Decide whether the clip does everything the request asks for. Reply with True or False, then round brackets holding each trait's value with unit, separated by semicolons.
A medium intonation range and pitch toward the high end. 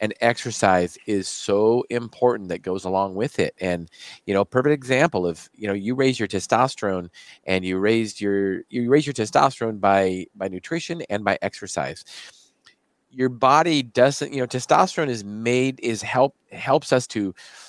False (5.0 semitones; 110 Hz)